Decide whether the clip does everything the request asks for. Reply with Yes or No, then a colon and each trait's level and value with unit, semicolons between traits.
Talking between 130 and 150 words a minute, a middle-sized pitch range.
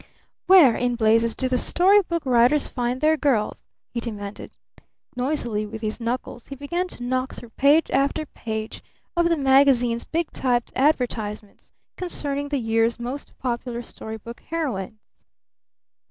Yes: average, 145 wpm; average, 3.7 semitones